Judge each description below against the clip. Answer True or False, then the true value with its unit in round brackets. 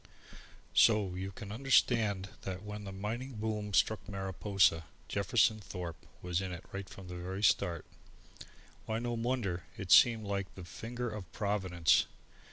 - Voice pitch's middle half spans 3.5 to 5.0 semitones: False (2.9 semitones)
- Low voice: True (100 Hz)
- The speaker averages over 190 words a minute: False (150 wpm)